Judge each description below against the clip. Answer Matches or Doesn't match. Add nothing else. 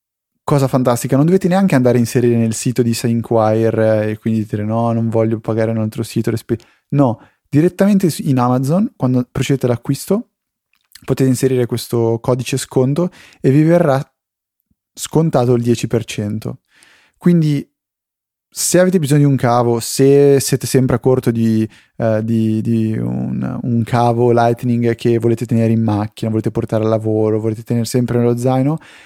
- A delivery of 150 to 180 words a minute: Matches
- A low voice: Matches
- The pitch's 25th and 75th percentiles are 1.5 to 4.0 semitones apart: Matches